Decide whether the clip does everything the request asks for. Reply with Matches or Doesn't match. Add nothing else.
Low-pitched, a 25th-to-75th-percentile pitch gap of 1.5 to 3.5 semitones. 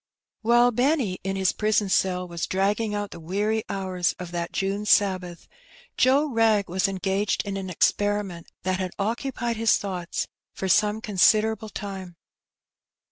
Doesn't match